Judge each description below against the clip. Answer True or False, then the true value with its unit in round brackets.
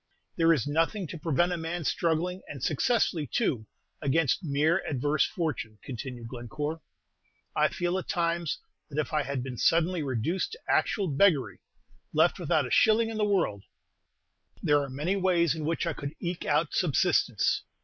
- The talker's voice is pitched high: False (160 Hz)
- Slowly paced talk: False (165 wpm)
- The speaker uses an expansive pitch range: False (3.9 semitones)